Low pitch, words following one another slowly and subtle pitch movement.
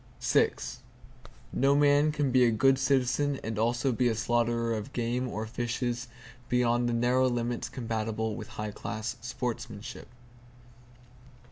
Yes: low, 120 Hz; slow, 130 wpm; narrow, 2.1 semitones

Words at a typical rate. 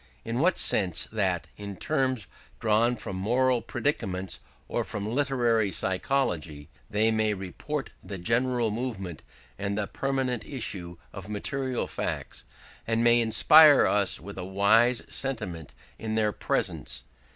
No: slow, 130 wpm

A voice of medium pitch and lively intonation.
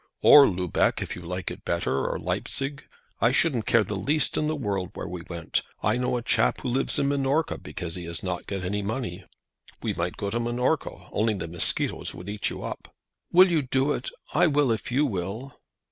No: low, 110 Hz; wide, 7.0 semitones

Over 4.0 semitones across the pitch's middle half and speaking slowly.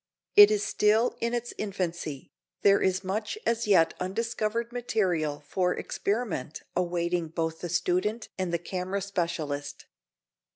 No: average, 3.7 semitones; slow, 130 wpm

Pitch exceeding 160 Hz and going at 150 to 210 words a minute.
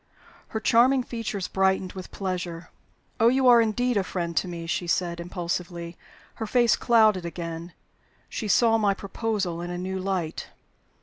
Yes: high, 190 Hz; average, 160 wpm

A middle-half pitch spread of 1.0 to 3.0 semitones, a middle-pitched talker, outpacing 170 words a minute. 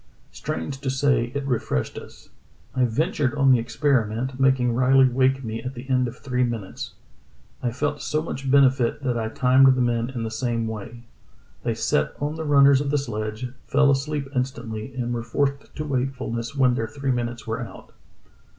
No: average, 2.7 semitones; low, 130 Hz; average, 185 wpm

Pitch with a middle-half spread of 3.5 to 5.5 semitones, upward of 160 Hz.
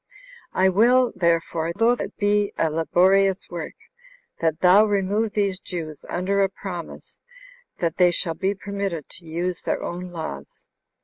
No: average, 3.0 semitones; medium, 185 Hz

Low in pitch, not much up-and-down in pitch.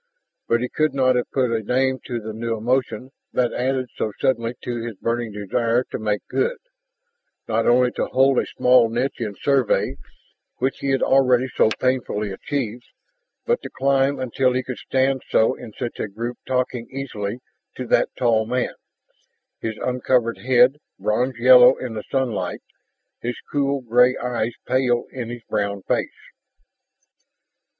Yes: low, 125 Hz; narrow, 2.2 semitones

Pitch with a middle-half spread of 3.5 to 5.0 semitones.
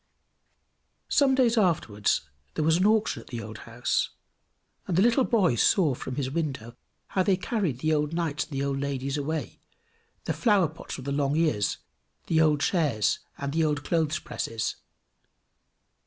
Yes: average, 4.7 semitones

